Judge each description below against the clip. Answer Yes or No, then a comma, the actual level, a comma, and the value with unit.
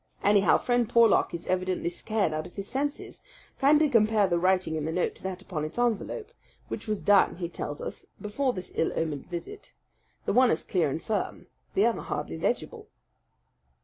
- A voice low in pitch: No, high, 195 Hz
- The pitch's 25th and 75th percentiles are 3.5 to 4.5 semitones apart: No, average, 5.3 semitones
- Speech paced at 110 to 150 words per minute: No, average, 185 wpm